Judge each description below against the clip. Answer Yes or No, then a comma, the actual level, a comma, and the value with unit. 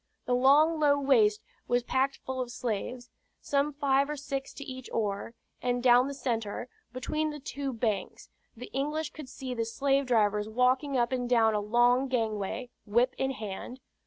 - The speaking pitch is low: No, very high, 250 Hz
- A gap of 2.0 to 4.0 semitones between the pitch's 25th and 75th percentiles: Yes, average, 3.0 semitones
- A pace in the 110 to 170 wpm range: No, average, 180 wpm